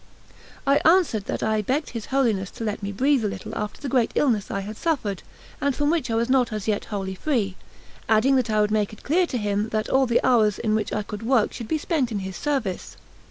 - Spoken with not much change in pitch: No, average, 4.3 semitones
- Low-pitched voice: No, high, 225 Hz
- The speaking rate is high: Yes, fast, 245 wpm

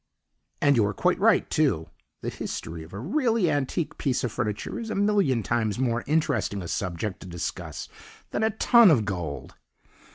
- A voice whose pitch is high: No, low, 120 Hz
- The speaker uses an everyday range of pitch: No, wide, 9.0 semitones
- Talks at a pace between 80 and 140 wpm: No, average, 175 wpm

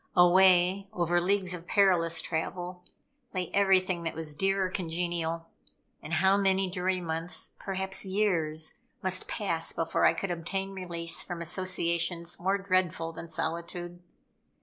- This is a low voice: No, medium, 180 Hz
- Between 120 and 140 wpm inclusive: Yes, slow, 135 wpm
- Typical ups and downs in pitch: No, narrow, 2.2 semitones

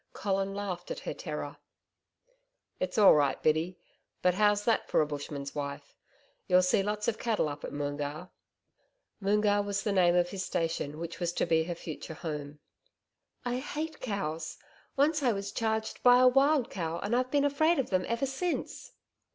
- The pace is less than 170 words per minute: No, average, 175 wpm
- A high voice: Yes, high, 195 Hz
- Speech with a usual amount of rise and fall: No, wide, 6.4 semitones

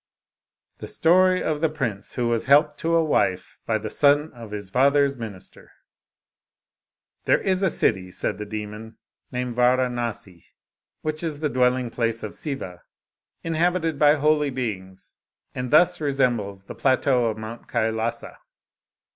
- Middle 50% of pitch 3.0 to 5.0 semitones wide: No, wide, 5.4 semitones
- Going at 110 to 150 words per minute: Yes, average, 140 wpm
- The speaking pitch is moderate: No, low, 125 Hz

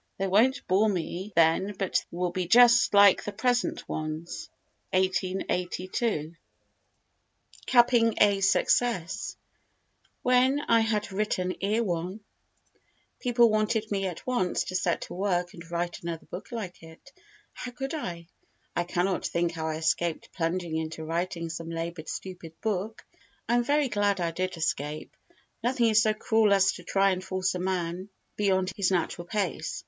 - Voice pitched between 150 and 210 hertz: Yes, medium, 185 Hz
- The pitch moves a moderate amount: Yes, average, 4.1 semitones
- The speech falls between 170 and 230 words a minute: No, average, 155 wpm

